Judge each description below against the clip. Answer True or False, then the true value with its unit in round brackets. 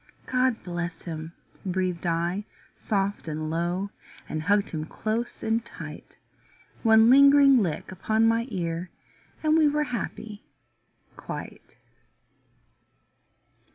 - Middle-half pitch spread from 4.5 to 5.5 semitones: True (5.2 semitones)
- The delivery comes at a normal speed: False (110 wpm)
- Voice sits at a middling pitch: False (200 Hz)